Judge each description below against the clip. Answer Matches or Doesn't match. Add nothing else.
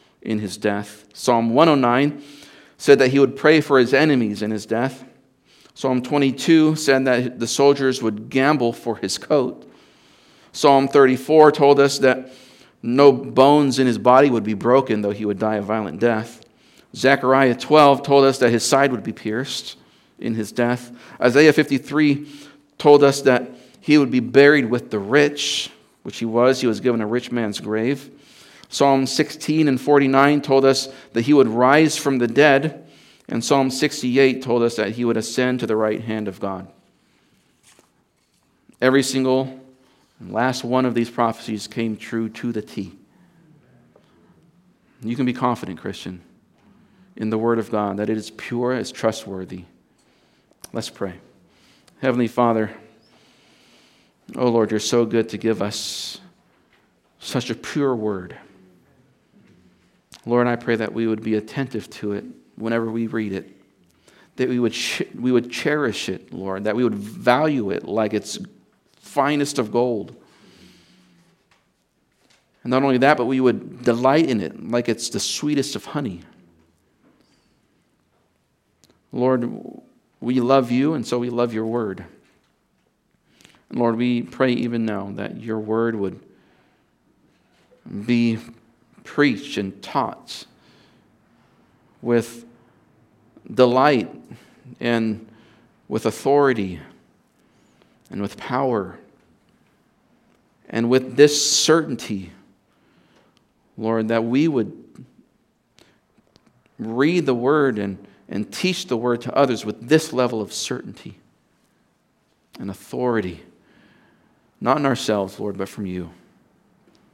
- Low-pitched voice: Matches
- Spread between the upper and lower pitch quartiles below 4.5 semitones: Matches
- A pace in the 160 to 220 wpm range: Doesn't match